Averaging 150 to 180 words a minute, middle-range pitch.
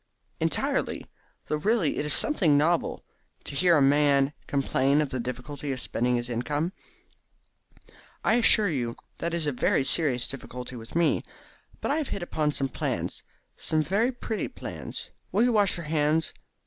Yes: average, 170 wpm; medium, 150 Hz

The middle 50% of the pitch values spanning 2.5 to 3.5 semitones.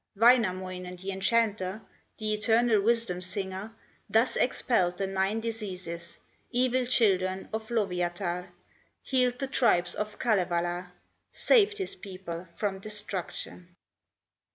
No: average, 4.0 semitones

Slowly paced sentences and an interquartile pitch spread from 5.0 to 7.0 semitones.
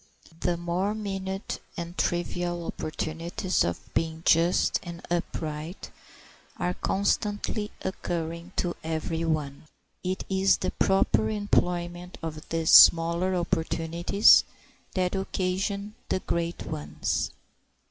No: slow, 105 wpm; narrow, 2.4 semitones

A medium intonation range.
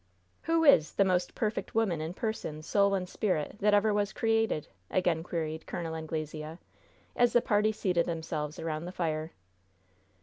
Yes: average, 4.8 semitones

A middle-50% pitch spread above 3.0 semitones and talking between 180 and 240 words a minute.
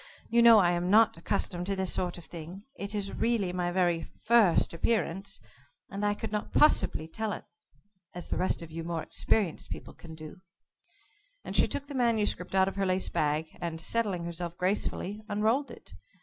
Yes: average, 3.5 semitones; average, 190 wpm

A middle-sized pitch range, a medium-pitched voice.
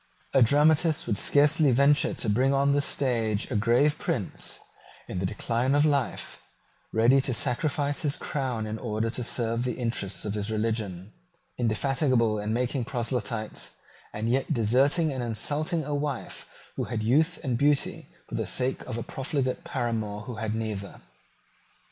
No: average, 4.2 semitones; low, 125 Hz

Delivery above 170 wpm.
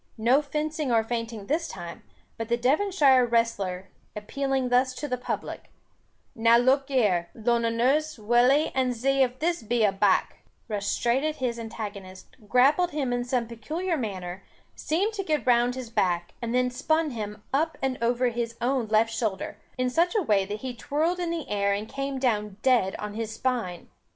Yes: average, 180 wpm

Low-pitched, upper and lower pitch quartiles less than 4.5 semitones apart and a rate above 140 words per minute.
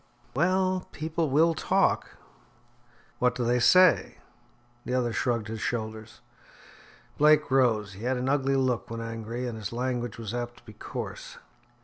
Yes: low, 125 Hz; average, 3.1 semitones; average, 150 wpm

